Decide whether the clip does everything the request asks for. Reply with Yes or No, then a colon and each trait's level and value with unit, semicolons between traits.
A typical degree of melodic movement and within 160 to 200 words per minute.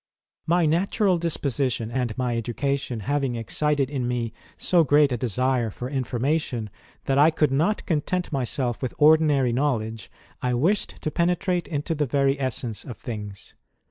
No: average, 4.1 semitones; average, 150 wpm